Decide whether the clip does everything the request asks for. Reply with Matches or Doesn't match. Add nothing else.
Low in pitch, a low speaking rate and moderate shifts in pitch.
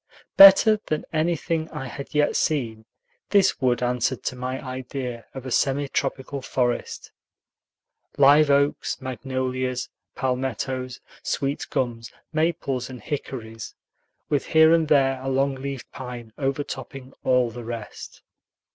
Doesn't match